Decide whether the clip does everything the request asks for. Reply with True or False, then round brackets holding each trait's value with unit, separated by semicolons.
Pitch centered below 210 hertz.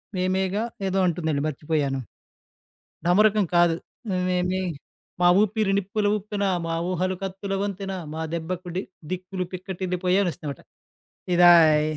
True (185 Hz)